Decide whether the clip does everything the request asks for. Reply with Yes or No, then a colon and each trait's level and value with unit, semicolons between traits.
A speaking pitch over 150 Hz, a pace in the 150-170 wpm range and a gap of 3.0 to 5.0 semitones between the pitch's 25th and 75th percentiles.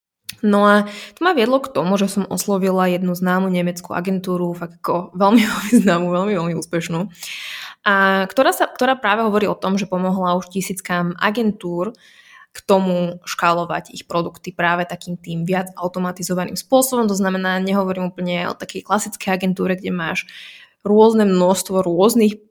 No: high, 190 Hz; average, 155 wpm; narrow, 2.4 semitones